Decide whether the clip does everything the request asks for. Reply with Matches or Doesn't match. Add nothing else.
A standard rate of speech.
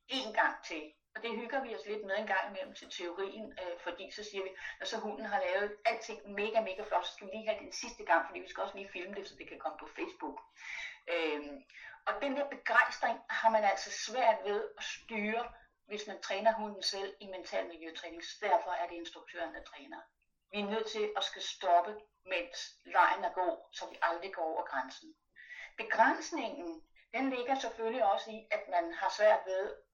Matches